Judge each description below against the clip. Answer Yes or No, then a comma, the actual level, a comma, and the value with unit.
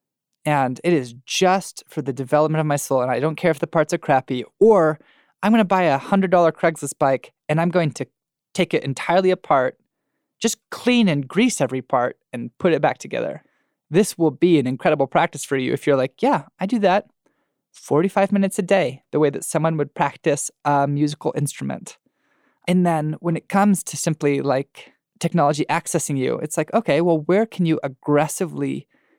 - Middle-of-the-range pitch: Yes, medium, 155 Hz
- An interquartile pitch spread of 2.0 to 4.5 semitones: Yes, average, 4.0 semitones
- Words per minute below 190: No, average, 195 wpm